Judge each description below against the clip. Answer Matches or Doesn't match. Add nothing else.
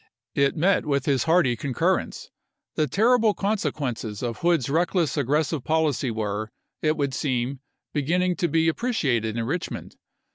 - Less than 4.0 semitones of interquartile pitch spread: Doesn't match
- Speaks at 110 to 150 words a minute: Matches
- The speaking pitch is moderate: Matches